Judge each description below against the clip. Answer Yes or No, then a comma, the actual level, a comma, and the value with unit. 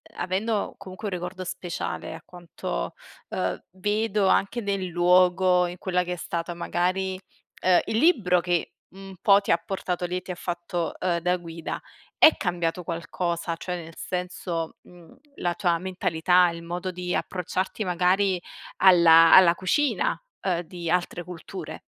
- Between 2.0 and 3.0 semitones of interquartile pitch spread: No, narrow, 1.5 semitones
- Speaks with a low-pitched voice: No, medium, 180 Hz